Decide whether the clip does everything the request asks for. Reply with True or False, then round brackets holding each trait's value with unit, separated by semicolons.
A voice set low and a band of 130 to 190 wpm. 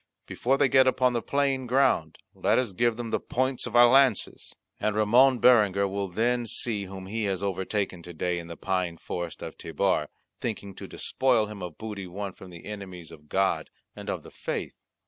False (105 Hz; 200 wpm)